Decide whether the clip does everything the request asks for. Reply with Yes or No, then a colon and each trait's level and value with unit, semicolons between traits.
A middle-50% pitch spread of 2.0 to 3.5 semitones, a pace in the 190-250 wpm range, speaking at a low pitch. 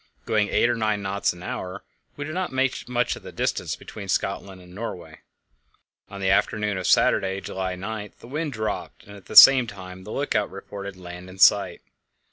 Yes: average, 3.1 semitones; average, 195 wpm; low, 100 Hz